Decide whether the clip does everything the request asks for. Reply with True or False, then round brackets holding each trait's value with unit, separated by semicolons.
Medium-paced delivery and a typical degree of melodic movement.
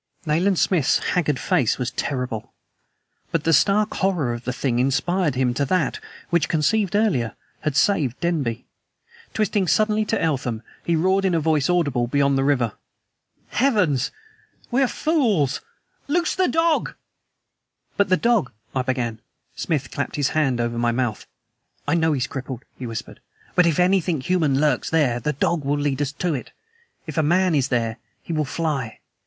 False (170 wpm; 5.8 semitones)